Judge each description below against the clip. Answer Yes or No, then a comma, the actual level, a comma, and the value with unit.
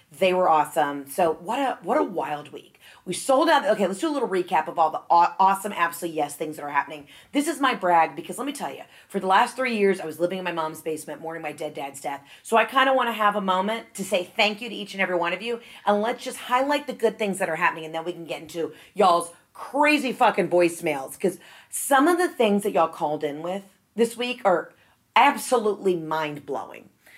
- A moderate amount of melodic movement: No, wide, 6.5 semitones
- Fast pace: Yes, fast, 245 wpm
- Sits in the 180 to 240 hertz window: Yes, high, 190 Hz